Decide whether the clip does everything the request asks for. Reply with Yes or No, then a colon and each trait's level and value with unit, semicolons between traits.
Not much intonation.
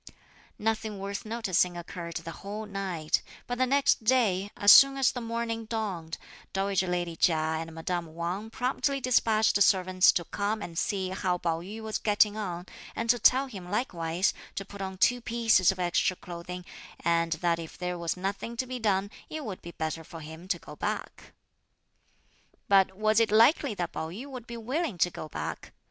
No: average, 4.4 semitones